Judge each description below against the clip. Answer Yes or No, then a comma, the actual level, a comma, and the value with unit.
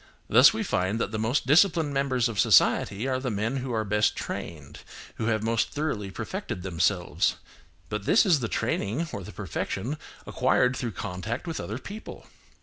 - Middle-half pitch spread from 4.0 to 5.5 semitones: Yes, average, 5.0 semitones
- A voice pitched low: Yes, low, 115 Hz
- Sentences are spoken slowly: No, average, 175 wpm